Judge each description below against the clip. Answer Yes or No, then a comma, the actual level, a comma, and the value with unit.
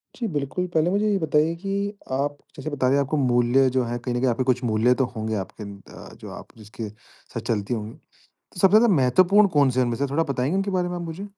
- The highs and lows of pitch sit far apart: Yes, wide, 6.2 semitones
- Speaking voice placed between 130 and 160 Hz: Yes, low, 135 Hz